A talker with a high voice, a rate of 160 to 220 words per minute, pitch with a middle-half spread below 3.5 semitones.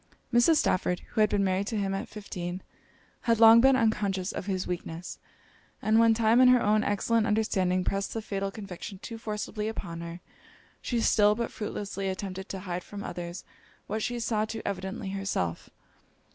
Yes: high, 205 Hz; average, 175 wpm; average, 2.9 semitones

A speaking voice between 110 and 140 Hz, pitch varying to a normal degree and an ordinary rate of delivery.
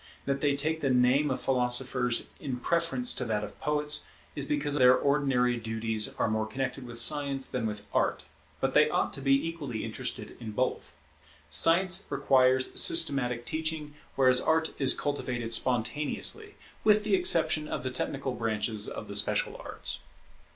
Yes: low, 135 Hz; average, 3.4 semitones; average, 160 wpm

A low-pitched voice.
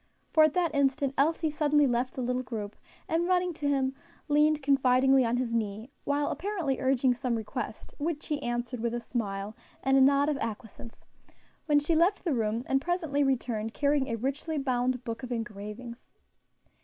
No: very high, 265 Hz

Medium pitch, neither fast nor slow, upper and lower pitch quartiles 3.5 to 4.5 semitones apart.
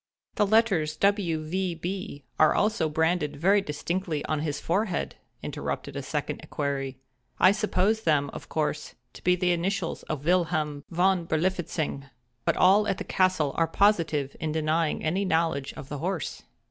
Yes: medium, 165 Hz; average, 155 wpm; average, 3.8 semitones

